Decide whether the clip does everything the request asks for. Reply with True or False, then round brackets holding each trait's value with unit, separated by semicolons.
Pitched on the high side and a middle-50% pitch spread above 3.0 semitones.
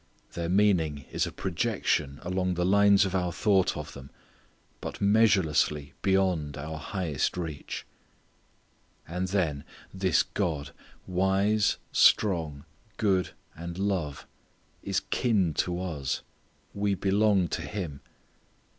False (90 Hz; 3.9 semitones)